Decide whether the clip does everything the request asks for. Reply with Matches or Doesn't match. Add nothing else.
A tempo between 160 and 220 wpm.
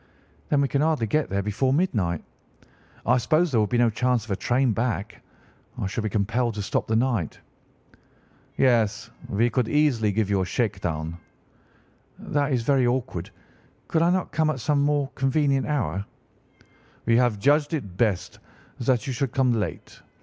Matches